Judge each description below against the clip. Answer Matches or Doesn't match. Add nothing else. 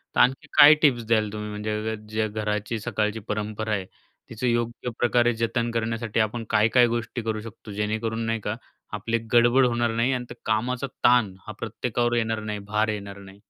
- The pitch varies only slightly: Matches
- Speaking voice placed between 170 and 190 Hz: Doesn't match